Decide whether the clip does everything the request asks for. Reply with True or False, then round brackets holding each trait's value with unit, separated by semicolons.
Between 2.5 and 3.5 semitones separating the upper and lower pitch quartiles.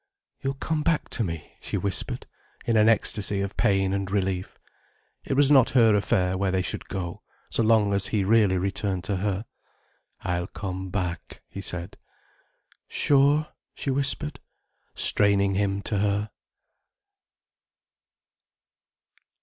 True (3.2 semitones)